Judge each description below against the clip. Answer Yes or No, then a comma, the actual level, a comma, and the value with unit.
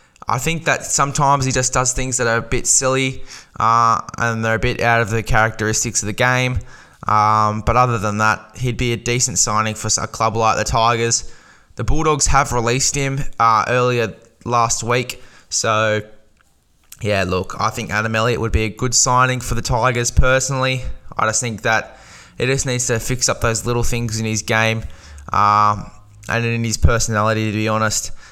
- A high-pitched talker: No, low, 115 Hz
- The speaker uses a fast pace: No, average, 190 wpm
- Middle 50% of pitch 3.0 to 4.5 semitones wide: No, narrow, 2.5 semitones